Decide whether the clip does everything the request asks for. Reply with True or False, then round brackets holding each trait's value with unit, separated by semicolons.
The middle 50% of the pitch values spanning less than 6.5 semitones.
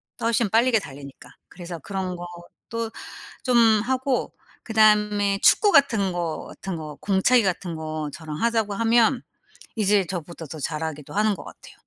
True (5.2 semitones)